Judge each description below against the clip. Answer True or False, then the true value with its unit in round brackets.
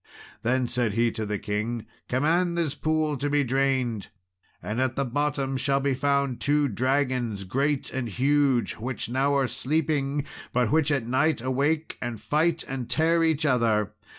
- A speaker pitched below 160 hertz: True (135 Hz)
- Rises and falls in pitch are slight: False (3.4 semitones)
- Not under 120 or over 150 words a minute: False (165 wpm)